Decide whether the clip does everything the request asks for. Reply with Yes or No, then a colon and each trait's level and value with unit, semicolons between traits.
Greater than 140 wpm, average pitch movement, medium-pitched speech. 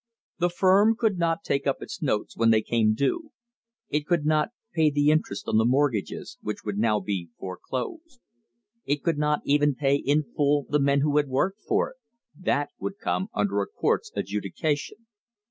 No: average, 180 wpm; wide, 6.4 semitones; medium, 145 Hz